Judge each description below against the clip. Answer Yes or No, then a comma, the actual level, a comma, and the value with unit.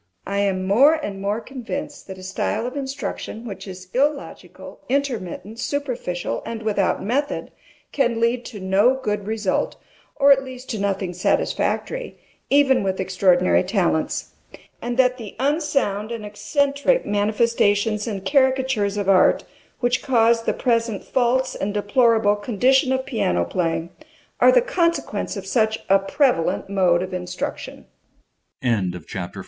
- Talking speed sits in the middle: No, slow, 120 wpm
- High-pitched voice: Yes, high, 225 Hz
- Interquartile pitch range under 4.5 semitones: No, average, 4.9 semitones